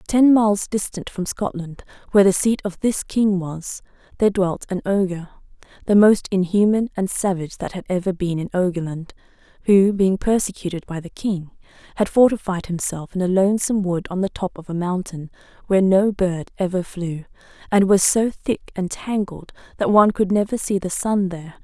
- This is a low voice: No, high, 190 Hz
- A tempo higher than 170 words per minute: Yes, average, 180 wpm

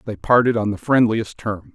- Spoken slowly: No, fast, 205 wpm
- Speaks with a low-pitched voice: Yes, low, 110 Hz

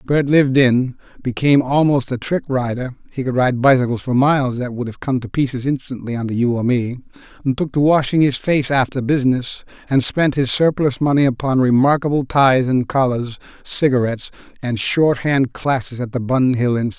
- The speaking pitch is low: Yes, low, 130 Hz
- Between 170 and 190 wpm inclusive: Yes, average, 175 wpm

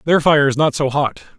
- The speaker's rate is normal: No, fast, 260 wpm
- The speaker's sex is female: No, male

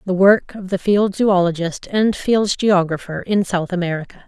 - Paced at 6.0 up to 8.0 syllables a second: No, 4.6 syllables/s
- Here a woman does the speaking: Yes, female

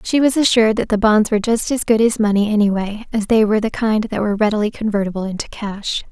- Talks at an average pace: No, fast, 235 wpm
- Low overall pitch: No, high, 215 Hz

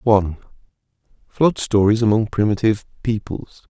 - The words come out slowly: Yes, slow, 95 wpm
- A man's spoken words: Yes, male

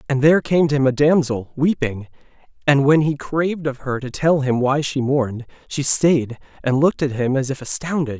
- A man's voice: Yes, male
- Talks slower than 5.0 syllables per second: No, 5.3 syllables/s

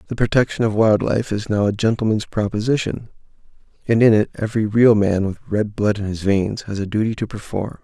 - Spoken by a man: Yes, male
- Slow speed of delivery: No, fast, 205 wpm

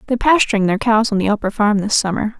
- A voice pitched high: Yes, high, 215 Hz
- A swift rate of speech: Yes, fast, 250 wpm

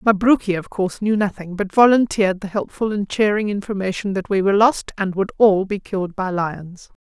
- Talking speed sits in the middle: Yes, average, 195 wpm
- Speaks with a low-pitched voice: No, high, 200 Hz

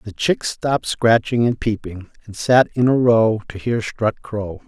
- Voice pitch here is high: No, low, 110 Hz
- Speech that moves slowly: No, average, 195 wpm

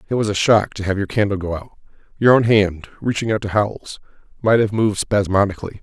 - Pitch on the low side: Yes, low, 100 Hz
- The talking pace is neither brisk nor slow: No, fast, 215 wpm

